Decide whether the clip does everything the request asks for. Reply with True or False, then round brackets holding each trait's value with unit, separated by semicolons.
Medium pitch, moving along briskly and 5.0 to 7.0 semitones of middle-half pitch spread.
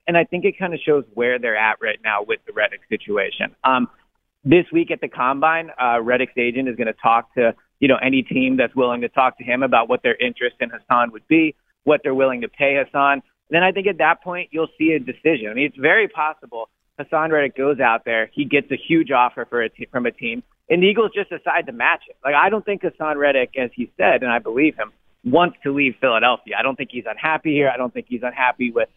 True (145 Hz; 255 wpm; 5.3 semitones)